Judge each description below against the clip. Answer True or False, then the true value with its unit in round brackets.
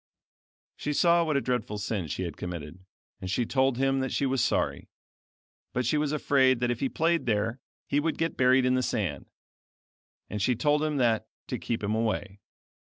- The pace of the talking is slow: False (195 wpm)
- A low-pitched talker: True (125 Hz)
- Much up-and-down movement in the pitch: False (4.5 semitones)